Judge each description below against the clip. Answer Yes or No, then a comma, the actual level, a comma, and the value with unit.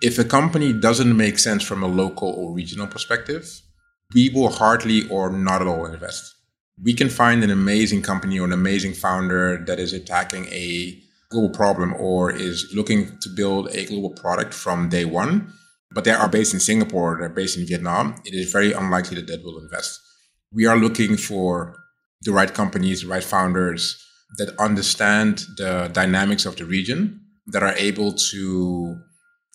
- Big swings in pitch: No, average, 4.3 semitones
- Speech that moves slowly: No, average, 175 wpm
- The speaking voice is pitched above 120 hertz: No, low, 100 Hz